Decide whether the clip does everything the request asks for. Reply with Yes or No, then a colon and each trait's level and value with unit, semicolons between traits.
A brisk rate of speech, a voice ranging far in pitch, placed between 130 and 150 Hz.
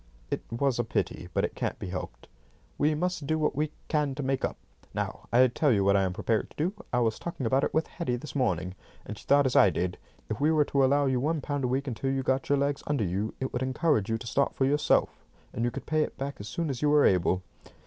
No: fast, 270 wpm; average, 4.5 semitones; low, 135 Hz